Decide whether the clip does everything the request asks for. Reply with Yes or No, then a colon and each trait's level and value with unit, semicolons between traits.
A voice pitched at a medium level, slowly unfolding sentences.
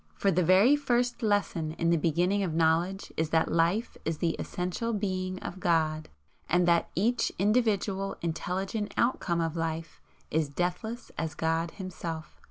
No: medium, 180 Hz; average, 155 wpm